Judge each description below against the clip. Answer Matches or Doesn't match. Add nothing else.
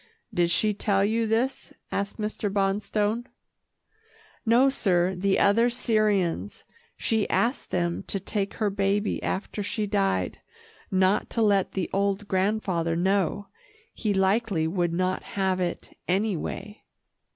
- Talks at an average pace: Doesn't match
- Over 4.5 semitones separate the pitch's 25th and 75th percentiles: Doesn't match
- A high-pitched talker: Matches